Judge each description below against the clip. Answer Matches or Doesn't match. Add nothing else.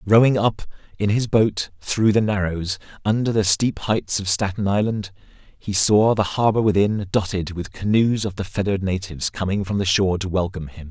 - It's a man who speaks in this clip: Matches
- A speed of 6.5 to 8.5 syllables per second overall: Doesn't match